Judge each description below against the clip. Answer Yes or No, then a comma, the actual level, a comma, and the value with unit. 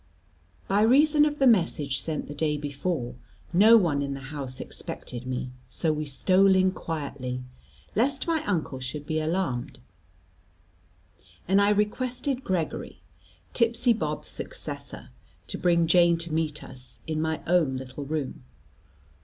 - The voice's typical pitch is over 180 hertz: No, medium, 160 Hz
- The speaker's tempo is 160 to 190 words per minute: No, average, 140 wpm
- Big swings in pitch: Yes, wide, 6.3 semitones